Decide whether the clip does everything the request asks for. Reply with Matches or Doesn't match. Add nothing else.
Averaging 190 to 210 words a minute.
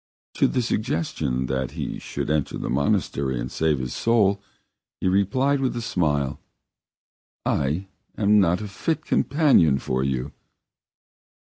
Doesn't match